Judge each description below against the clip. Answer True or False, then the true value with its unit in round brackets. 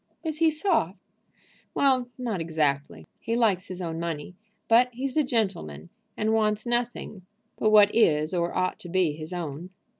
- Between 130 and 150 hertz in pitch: False (195 Hz)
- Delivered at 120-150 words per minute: False (160 wpm)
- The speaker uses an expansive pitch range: True (6.6 semitones)